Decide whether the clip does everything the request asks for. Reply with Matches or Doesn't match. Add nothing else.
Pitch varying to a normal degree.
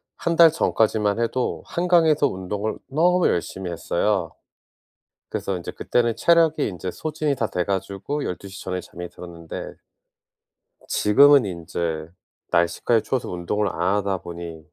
Doesn't match